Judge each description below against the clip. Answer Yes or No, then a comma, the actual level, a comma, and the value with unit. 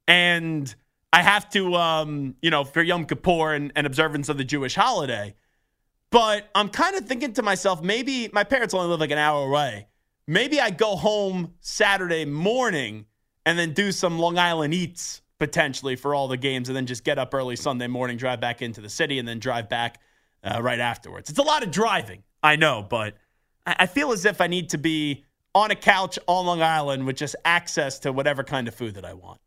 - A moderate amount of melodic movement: No, wide, 5.8 semitones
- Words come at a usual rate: No, fast, 210 wpm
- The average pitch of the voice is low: No, medium, 155 Hz